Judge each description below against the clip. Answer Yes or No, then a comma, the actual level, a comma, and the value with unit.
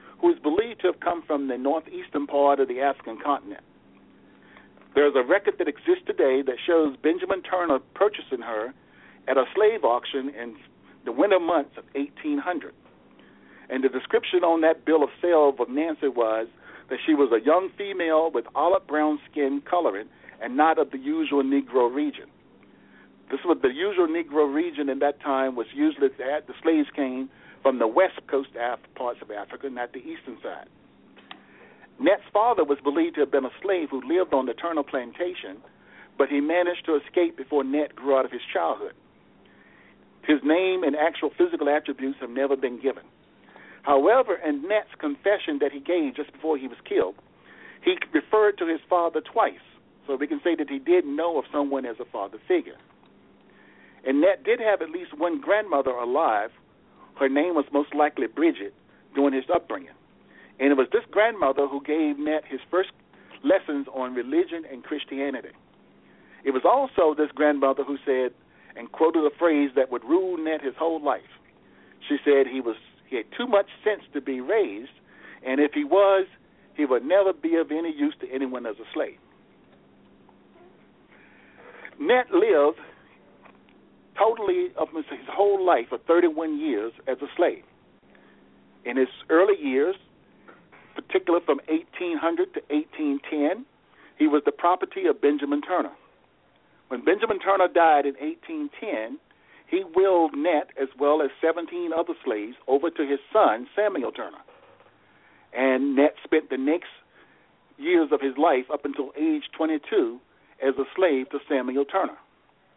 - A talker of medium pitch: Yes, medium, 160 Hz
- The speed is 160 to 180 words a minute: Yes, average, 165 wpm